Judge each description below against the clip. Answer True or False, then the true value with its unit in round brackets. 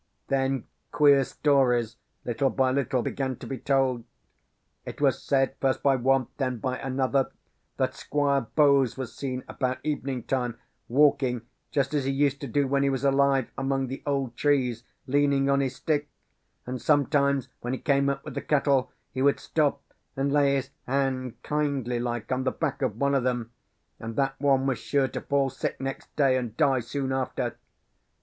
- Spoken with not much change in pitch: True (1.4 semitones)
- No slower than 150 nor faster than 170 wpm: False (180 wpm)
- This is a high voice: False (135 Hz)